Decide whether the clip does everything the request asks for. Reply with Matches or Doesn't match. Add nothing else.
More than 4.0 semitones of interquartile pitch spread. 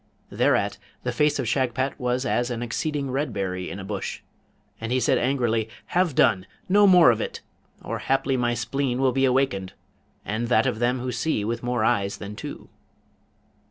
Doesn't match